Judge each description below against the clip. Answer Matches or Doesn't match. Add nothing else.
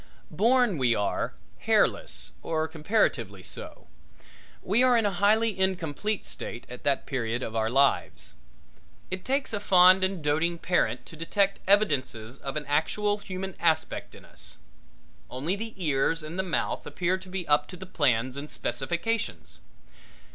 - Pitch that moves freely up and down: Matches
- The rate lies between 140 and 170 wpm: Matches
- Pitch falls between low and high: Matches